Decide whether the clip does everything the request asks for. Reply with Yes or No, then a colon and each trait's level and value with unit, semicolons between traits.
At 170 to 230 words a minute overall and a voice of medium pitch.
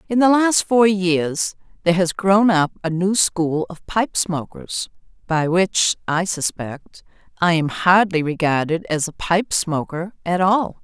No: average, 160 wpm; medium, 180 Hz